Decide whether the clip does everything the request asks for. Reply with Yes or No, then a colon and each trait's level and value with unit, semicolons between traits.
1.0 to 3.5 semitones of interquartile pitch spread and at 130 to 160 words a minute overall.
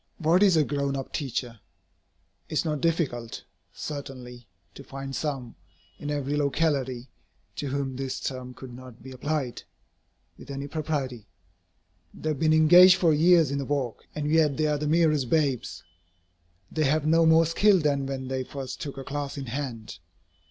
No: average, 2.9 semitones; average, 170 wpm